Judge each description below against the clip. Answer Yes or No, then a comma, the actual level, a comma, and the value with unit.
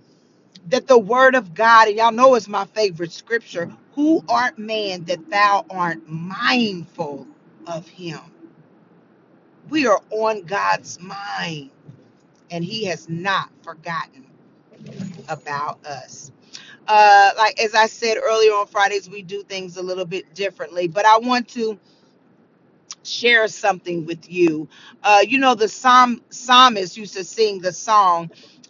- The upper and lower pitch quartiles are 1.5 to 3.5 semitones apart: No, average, 4.3 semitones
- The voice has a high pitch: Yes, high, 200 Hz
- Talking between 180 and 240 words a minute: No, average, 140 wpm